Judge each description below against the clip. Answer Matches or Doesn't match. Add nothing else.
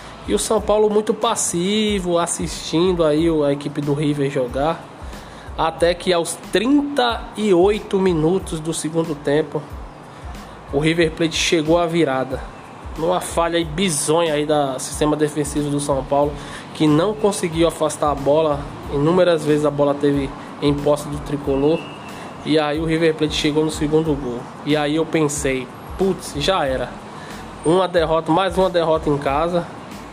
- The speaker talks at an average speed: Matches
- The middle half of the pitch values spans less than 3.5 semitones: Matches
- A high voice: Doesn't match